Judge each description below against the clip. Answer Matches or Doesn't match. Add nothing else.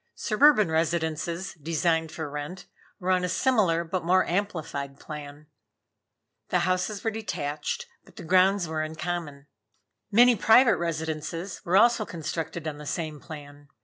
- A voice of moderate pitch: Matches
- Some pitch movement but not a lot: Matches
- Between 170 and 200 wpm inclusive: Doesn't match